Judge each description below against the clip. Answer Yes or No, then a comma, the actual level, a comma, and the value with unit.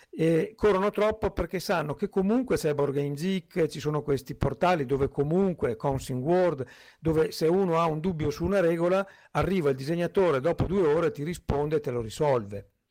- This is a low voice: No, medium, 160 Hz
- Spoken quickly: Yes, fast, 180 wpm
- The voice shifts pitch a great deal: No, average, 4.9 semitones